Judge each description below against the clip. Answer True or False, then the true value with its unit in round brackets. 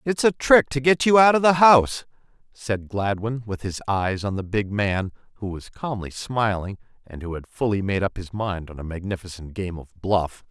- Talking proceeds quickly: True (210 wpm)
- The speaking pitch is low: True (110 Hz)